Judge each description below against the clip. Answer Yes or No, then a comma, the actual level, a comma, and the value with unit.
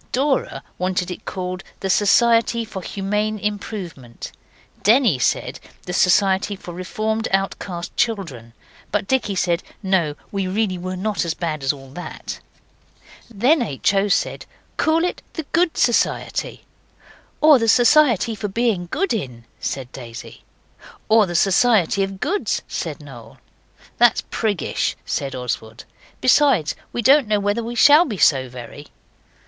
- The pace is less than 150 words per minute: Yes, average, 140 wpm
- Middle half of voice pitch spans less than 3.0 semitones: No, average, 4.9 semitones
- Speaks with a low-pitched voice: No, high, 195 Hz